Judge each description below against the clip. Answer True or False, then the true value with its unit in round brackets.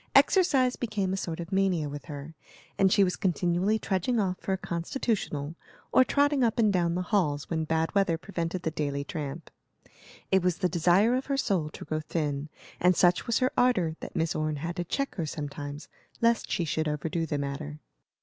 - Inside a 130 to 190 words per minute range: False (200 wpm)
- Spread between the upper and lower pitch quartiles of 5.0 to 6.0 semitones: False (4.4 semitones)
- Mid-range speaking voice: True (175 Hz)